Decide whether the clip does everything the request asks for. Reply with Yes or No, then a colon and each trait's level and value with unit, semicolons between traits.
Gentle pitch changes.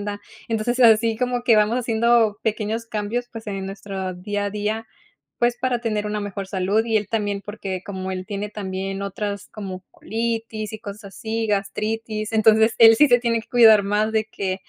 Yes: narrow, 2.1 semitones